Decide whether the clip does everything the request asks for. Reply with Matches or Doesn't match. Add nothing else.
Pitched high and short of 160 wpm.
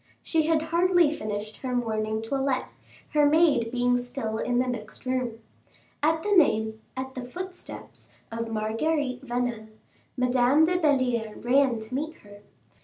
Matches